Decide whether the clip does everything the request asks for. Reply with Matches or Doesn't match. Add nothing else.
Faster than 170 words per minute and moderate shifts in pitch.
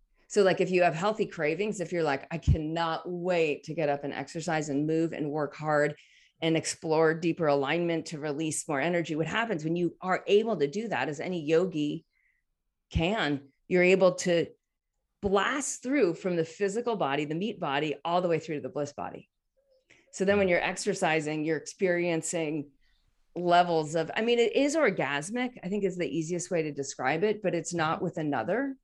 Matches